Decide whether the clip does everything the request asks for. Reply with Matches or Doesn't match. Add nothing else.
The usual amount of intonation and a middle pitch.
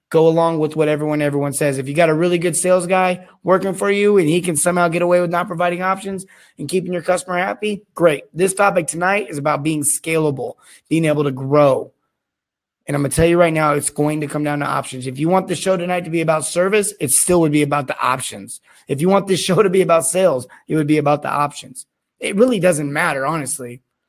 Matches